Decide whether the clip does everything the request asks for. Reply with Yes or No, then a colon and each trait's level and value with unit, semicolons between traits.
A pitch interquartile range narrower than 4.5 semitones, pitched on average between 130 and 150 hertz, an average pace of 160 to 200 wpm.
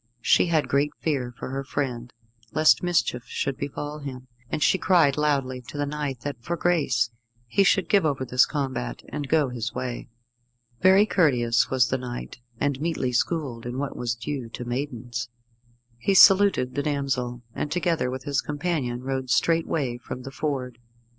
Yes: average, 3.5 semitones; low, 135 Hz; average, 170 wpm